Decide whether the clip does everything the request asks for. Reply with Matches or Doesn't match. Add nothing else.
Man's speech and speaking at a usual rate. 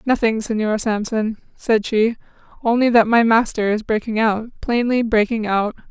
Doesn't match